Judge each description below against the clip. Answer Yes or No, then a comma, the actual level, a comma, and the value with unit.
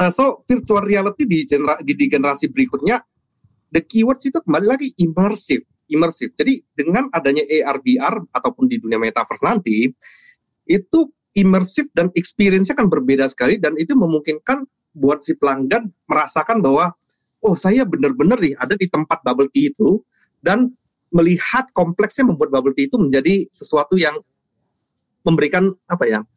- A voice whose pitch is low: No, medium, 185 Hz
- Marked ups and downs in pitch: Yes, wide, 8.3 semitones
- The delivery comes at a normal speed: No, fast, 145 wpm